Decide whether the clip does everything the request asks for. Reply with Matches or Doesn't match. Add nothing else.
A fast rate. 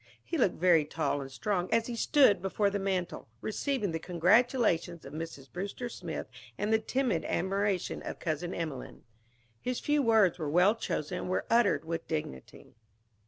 Doesn't match